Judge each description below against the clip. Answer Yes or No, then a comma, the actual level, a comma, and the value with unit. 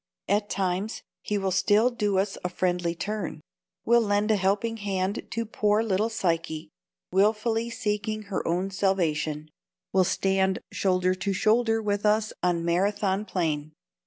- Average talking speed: Yes, average, 145 wpm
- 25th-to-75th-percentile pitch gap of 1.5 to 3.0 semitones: Yes, narrow, 2.6 semitones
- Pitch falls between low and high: No, high, 195 Hz